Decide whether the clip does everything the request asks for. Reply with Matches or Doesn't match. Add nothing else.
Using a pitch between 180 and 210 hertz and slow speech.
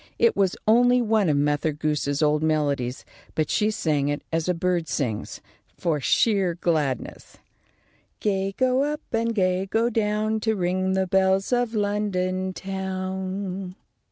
Doesn't match